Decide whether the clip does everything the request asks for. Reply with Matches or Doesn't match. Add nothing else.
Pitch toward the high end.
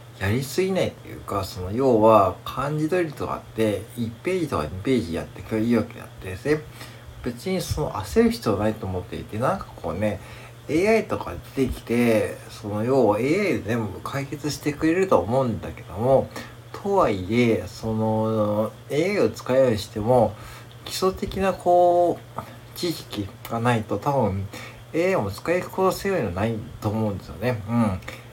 Doesn't match